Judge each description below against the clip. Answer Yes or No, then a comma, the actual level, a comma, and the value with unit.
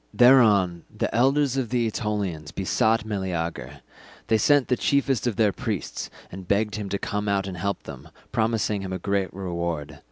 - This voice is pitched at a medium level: No, low, 105 Hz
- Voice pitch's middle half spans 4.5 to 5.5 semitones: No, average, 3.6 semitones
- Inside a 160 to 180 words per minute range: Yes, average, 170 wpm